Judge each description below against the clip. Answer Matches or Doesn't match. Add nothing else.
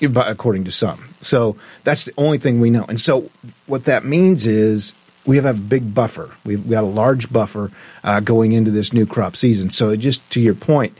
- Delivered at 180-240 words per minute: Matches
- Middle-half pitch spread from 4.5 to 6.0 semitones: Doesn't match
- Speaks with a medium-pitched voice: Doesn't match